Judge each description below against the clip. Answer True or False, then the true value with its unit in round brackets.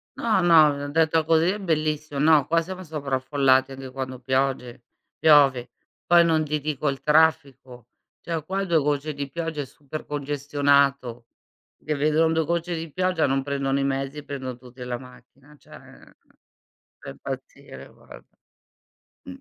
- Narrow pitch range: False (3.0 semitones)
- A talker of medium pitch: True (145 Hz)